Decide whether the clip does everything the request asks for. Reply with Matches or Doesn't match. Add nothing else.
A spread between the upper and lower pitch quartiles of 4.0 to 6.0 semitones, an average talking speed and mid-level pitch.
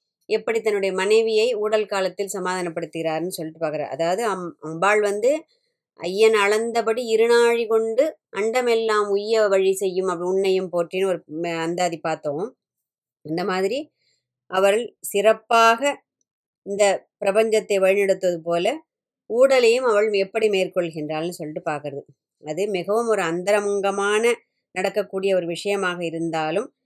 Doesn't match